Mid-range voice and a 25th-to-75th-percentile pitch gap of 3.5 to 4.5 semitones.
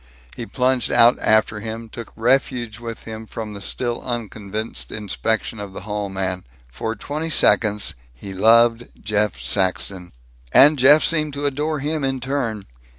No: low, 115 Hz; average, 3.9 semitones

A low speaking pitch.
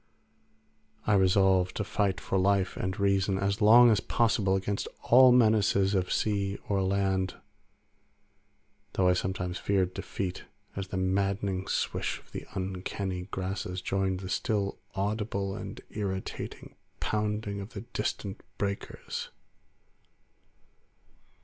Yes: low, 100 Hz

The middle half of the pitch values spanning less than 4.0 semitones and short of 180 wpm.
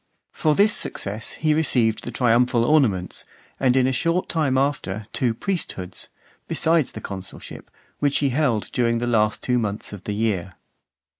No: average, 5.2 semitones; average, 160 wpm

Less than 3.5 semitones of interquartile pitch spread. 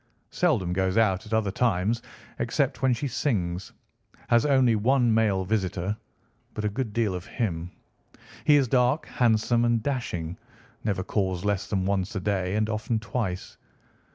No: average, 3.9 semitones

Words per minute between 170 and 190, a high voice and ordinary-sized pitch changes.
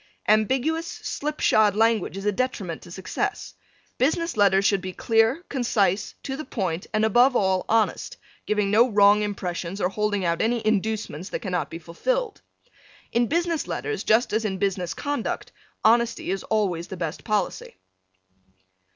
No: average, 155 wpm; high, 215 Hz; average, 4.1 semitones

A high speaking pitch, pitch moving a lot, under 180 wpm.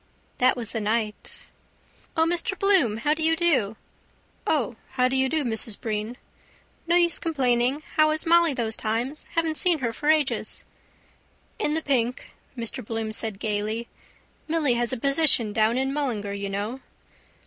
Yes: very high, 255 Hz; wide, 5.7 semitones; average, 160 wpm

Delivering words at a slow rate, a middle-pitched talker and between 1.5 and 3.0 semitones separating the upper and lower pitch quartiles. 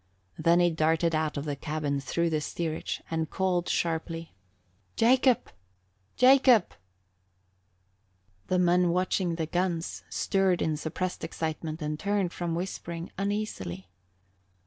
Yes: slow, 125 wpm; medium, 170 Hz; average, 2.7 semitones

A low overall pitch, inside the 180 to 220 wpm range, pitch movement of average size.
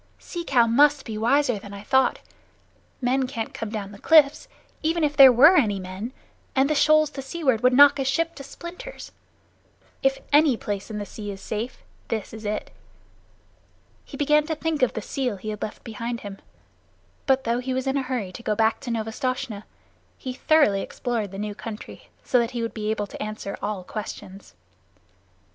No: high, 240 Hz; average, 195 wpm; average, 4.6 semitones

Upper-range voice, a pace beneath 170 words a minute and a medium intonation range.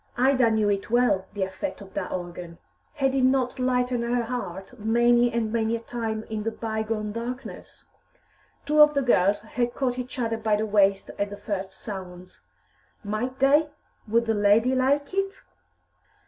No: high, 230 Hz; average, 175 wpm; average, 3.5 semitones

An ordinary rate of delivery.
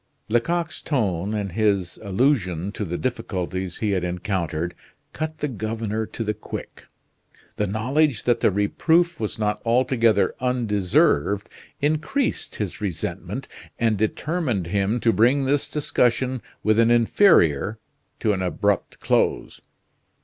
No: slow, 125 wpm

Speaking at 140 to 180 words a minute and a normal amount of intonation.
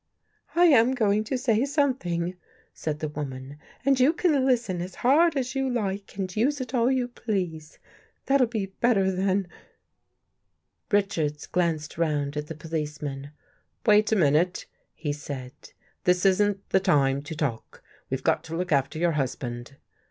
No: average, 170 wpm; wide, 8.0 semitones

